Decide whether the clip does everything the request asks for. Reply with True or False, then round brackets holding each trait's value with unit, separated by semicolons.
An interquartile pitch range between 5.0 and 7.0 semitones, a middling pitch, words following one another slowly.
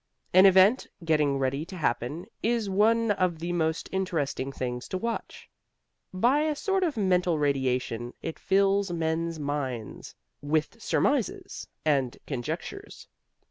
True (5.6 semitones; 165 Hz; 130 wpm)